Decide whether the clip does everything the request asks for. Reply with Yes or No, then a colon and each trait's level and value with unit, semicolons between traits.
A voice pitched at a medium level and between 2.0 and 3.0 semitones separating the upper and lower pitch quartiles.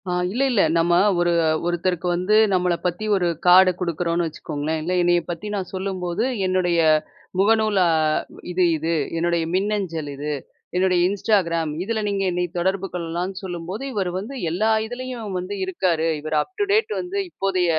Yes: medium, 180 Hz; average, 2.7 semitones